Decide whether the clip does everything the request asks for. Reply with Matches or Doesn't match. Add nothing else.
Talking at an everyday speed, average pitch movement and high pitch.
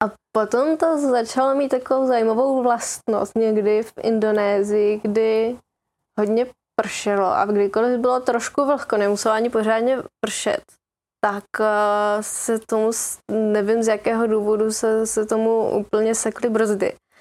Doesn't match